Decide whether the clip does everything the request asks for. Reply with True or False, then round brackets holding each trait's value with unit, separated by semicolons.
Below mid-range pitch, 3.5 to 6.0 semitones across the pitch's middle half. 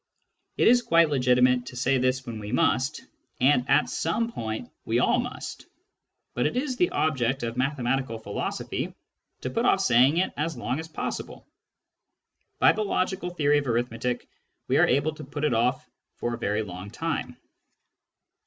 True (130 Hz; 4.5 semitones)